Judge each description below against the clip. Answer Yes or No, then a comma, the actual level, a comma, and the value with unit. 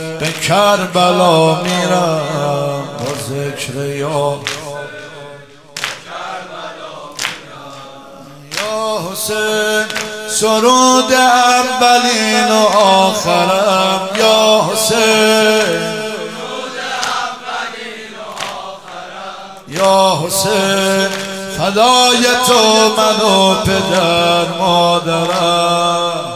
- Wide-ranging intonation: No, average, 4.6 semitones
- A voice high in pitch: Yes, high, 195 Hz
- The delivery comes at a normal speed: No, slow, 50 wpm